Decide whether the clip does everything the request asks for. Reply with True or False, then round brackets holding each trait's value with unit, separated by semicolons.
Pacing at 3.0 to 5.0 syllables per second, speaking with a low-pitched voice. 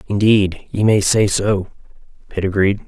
True (4.3 syllables/s; 100 Hz)